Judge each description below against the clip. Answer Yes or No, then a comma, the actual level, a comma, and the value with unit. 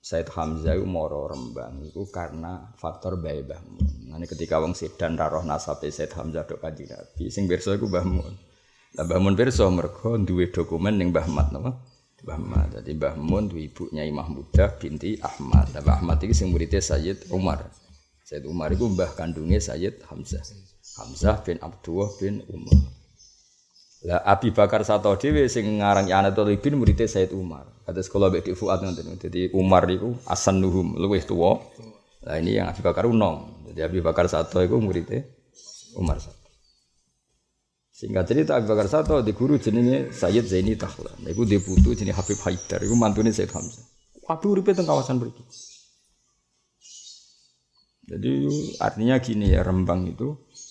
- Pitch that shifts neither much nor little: Yes, average, 4.7 semitones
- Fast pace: Yes, fast, 160 wpm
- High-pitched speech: No, very low, 95 Hz